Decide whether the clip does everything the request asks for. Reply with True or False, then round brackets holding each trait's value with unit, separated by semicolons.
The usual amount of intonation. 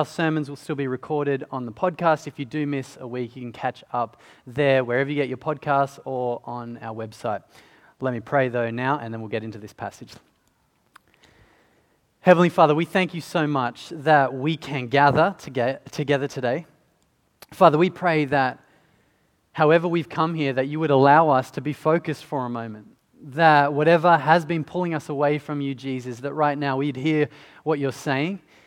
True (3.4 semitones)